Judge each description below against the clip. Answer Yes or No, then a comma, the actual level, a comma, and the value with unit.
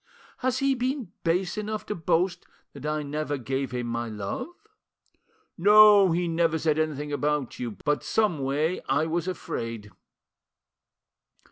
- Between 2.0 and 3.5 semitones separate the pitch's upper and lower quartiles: No, average, 5.2 semitones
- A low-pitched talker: No, medium, 155 Hz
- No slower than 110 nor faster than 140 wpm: Yes, slow, 135 wpm